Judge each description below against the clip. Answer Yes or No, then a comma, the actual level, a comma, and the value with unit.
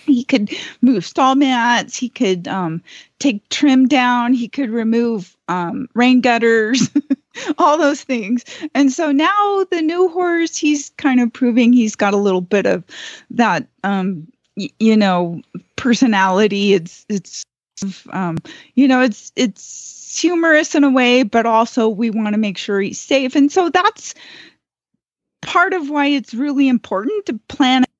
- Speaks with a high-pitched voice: Yes, very high, 250 Hz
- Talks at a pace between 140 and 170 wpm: Yes, average, 155 wpm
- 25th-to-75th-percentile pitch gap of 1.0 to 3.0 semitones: No, average, 4.8 semitones